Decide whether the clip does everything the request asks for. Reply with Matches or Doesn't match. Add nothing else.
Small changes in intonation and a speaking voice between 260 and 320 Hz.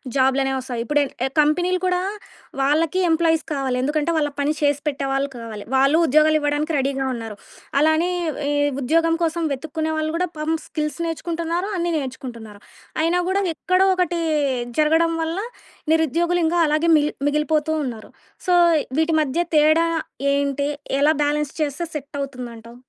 Doesn't match